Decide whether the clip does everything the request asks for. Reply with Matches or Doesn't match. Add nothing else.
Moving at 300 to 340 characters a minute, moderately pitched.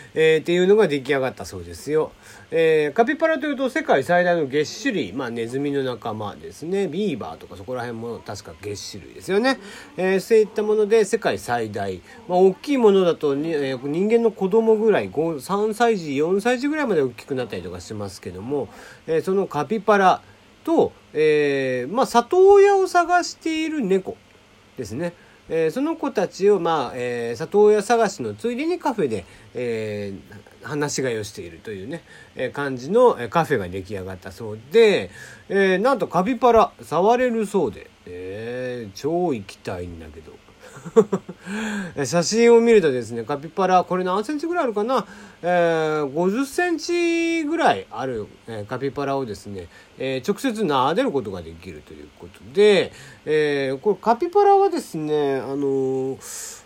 Matches